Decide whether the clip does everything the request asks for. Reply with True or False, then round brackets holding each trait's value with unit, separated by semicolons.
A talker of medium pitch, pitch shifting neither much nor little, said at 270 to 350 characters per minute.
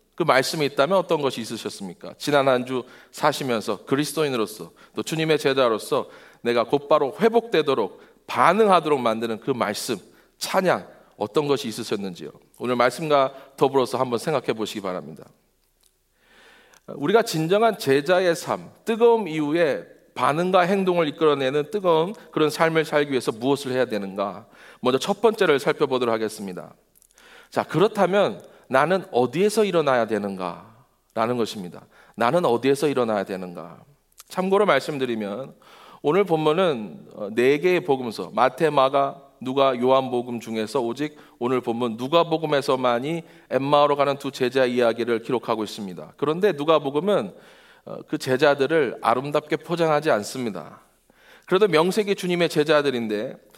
True (145 Hz; 4.9 semitones; 335 characters per minute)